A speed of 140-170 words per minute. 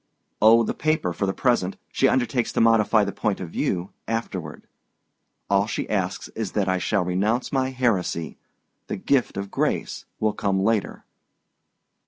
Yes: average, 160 wpm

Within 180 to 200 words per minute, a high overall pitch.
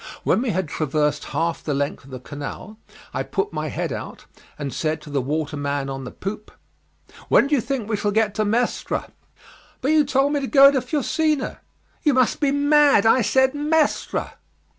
Yes: average, 190 wpm; high, 220 Hz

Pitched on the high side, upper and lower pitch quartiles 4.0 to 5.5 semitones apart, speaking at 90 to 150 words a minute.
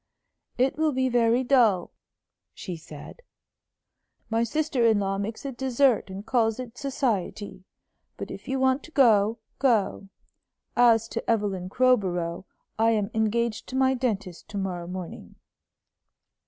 Yes: high, 225 Hz; average, 4.5 semitones; average, 140 wpm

